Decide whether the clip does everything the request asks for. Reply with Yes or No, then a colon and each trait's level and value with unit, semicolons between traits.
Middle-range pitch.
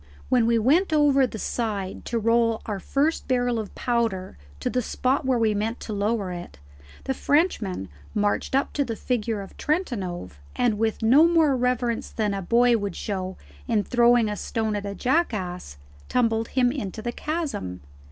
No: high, 230 Hz